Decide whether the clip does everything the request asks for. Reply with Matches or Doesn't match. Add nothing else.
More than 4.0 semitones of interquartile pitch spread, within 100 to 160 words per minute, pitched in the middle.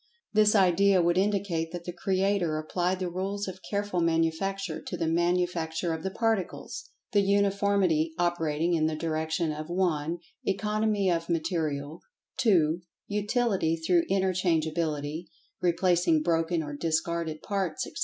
Doesn't match